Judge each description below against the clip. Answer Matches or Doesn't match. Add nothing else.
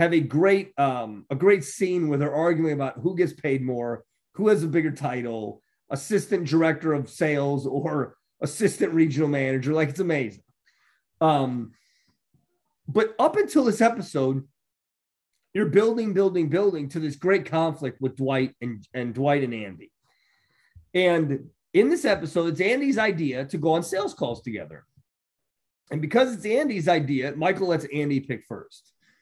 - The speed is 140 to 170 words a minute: Matches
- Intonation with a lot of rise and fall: Matches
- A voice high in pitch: Doesn't match